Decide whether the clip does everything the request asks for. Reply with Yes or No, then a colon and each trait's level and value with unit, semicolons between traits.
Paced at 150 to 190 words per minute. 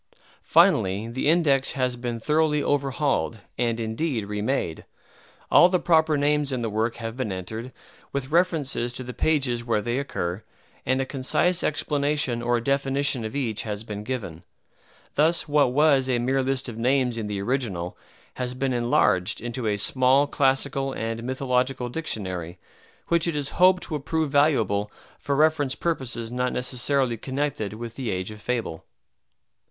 Yes: average, 160 wpm